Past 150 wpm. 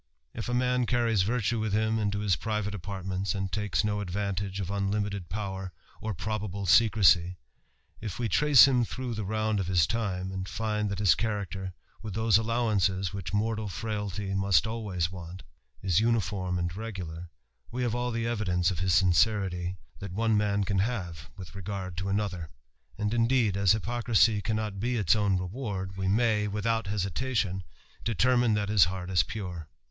Yes: average, 170 wpm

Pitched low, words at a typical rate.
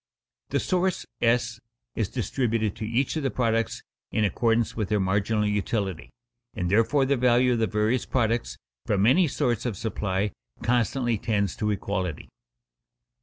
Yes: low, 115 Hz; average, 150 wpm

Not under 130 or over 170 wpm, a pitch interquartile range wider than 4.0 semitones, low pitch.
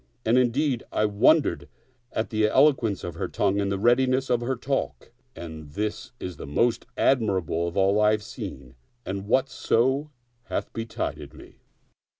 Yes: average, 165 wpm; average, 4.4 semitones; low, 110 Hz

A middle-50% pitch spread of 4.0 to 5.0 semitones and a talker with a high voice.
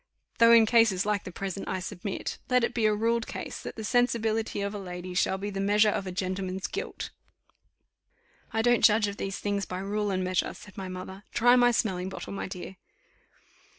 No: average, 2.9 semitones; high, 200 Hz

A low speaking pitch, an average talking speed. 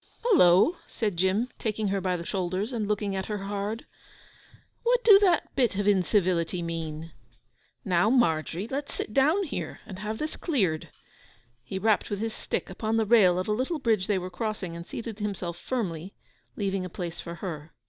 No: high, 200 Hz; average, 180 wpm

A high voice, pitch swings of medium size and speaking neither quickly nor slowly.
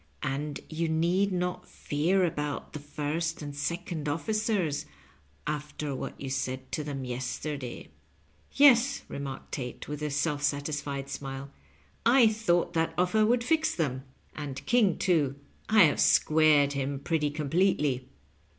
No: medium, 150 Hz; average, 4.1 semitones; average, 145 wpm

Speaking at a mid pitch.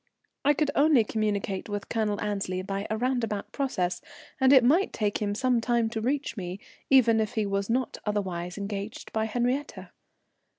No: high, 220 Hz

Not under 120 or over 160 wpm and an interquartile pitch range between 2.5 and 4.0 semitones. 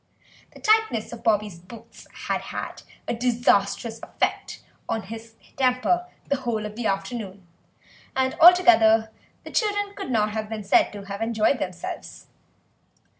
Yes: slow, 135 wpm; average, 3.7 semitones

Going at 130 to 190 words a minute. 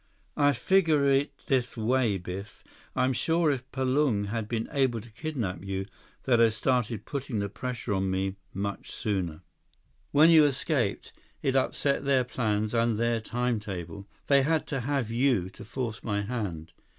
Yes: average, 160 wpm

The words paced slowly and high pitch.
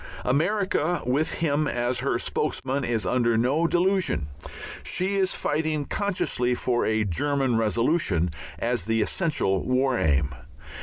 No: slow, 125 wpm; low, 130 Hz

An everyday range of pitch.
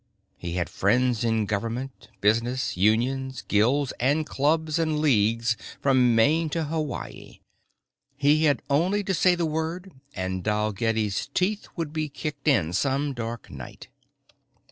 No: wide, 5.7 semitones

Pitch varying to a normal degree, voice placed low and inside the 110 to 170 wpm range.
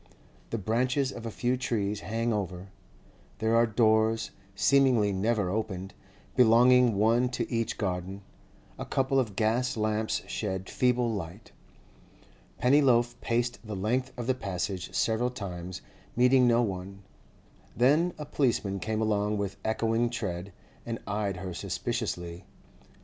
Yes: average, 3.6 semitones; low, 110 Hz; slow, 135 wpm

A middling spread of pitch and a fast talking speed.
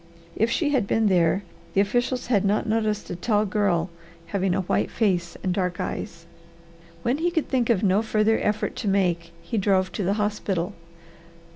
No: average, 3.1 semitones; average, 180 wpm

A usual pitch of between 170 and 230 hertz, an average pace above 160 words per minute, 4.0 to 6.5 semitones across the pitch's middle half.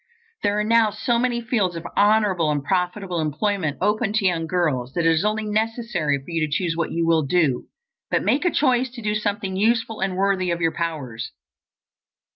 Yes: high, 190 Hz; average, 200 wpm; average, 4.7 semitones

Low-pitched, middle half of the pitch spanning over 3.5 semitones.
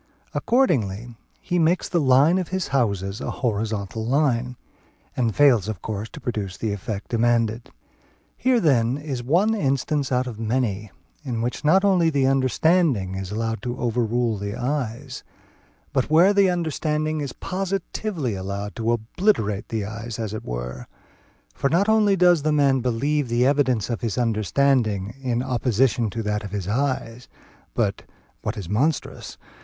Yes: low, 125 Hz; wide, 5.5 semitones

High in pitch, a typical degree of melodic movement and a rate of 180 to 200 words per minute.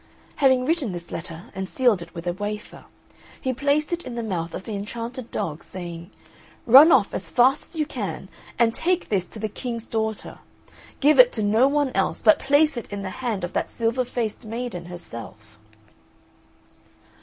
No: high, 225 Hz; wide, 5.9 semitones; average, 185 wpm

